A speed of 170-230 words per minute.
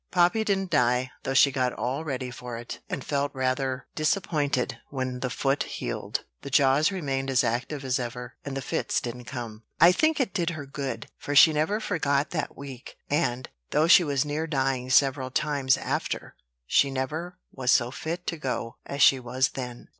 Yes: average, 185 wpm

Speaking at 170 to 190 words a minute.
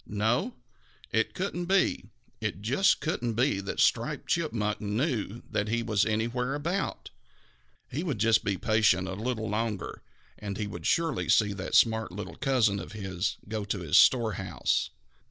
No: average, 155 wpm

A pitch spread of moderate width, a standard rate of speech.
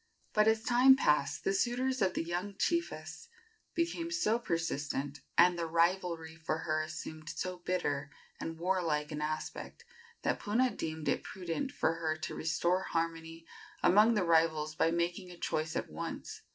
Yes: average, 4.2 semitones; average, 160 wpm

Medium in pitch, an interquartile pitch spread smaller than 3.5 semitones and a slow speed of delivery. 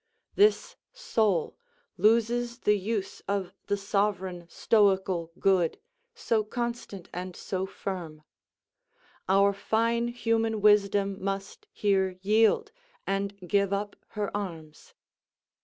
No: high, 200 Hz; average, 2.7 semitones; slow, 105 wpm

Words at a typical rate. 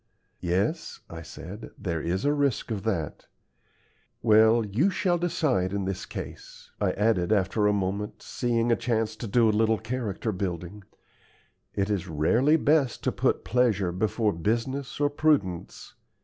Yes: average, 150 wpm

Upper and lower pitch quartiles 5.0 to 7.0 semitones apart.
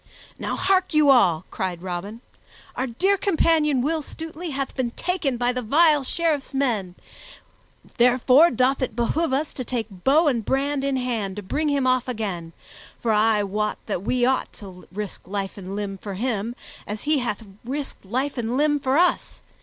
Yes: wide, 5.6 semitones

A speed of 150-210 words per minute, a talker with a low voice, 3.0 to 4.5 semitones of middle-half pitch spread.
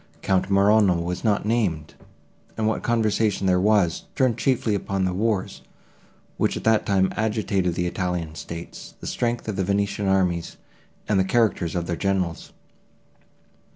Yes: average, 155 wpm; low, 100 Hz; average, 3.3 semitones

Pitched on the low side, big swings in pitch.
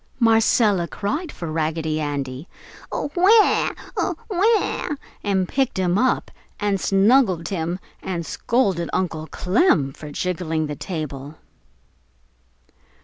No: medium, 180 Hz; wide, 6.2 semitones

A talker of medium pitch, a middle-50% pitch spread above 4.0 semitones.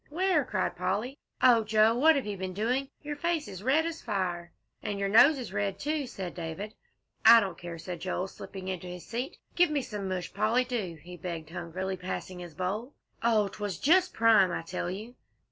No: high, 205 Hz; wide, 5.6 semitones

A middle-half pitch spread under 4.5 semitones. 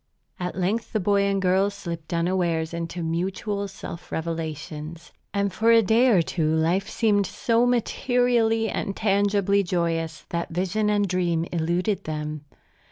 Yes: average, 3.5 semitones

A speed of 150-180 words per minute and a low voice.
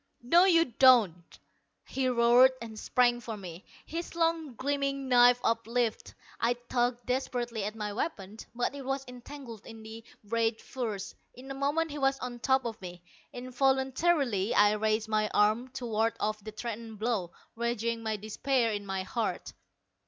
No: average, 160 wpm; high, 235 Hz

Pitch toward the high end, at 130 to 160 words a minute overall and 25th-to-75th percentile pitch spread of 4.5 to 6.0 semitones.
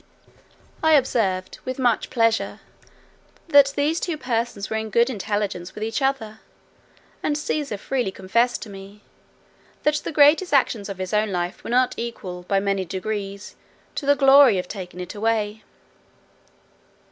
Yes: high, 220 Hz; average, 150 wpm; average, 5.3 semitones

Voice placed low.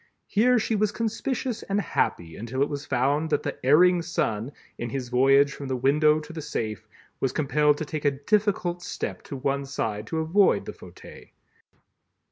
No: medium, 145 Hz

